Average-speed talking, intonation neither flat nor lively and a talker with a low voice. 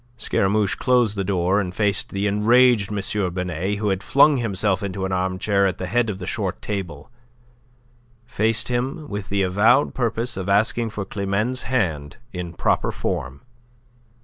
Yes: average, 160 wpm; average, 3.2 semitones; low, 100 Hz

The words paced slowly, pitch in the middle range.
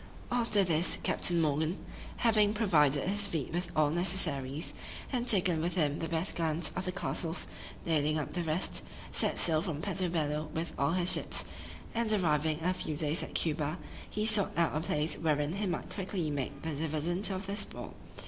No: average, 185 wpm; medium, 165 Hz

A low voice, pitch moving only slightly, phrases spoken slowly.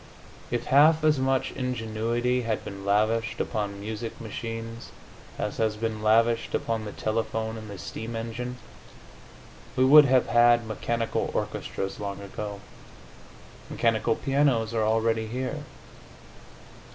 Yes: low, 115 Hz; narrow, 1.9 semitones; slow, 125 wpm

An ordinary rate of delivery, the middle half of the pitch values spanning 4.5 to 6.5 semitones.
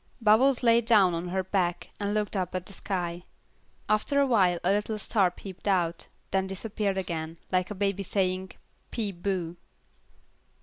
No: average, 165 wpm; average, 2.8 semitones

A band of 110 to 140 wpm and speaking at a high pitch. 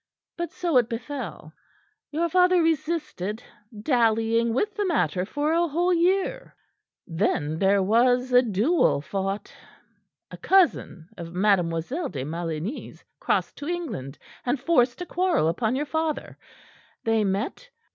Yes: slow, 135 wpm; high, 245 Hz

